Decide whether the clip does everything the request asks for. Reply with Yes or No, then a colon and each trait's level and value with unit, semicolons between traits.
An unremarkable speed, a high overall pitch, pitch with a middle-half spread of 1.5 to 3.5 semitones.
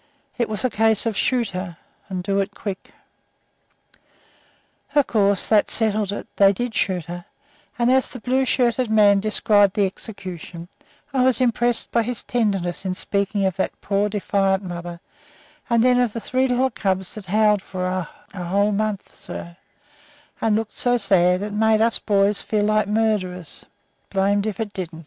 Yes: average, 170 wpm; high, 205 Hz; average, 2.8 semitones